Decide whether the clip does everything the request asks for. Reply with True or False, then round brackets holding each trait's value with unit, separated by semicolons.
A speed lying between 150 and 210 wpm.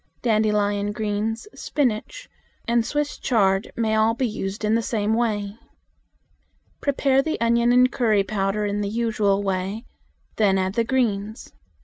False (135 wpm)